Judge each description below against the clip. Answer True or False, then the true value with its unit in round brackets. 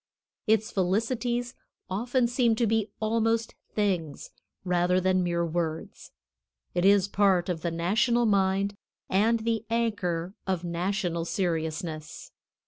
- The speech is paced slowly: True (120 wpm)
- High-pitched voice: True (195 Hz)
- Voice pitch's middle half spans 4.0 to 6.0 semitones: True (4.3 semitones)